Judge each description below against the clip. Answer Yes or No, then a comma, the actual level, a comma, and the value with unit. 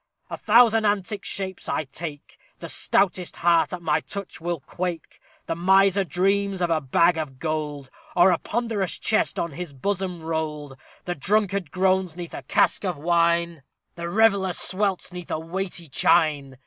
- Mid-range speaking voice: Yes, medium, 175 Hz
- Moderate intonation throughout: Yes, average, 3.3 semitones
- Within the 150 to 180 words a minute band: Yes, average, 165 wpm